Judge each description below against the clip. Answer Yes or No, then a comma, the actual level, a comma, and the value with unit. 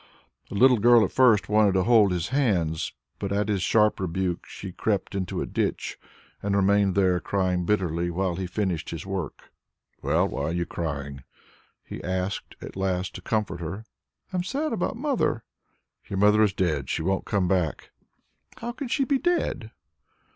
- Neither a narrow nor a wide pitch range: Yes, average, 3.4 semitones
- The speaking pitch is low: Yes, very low, 95 Hz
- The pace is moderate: Yes, average, 175 wpm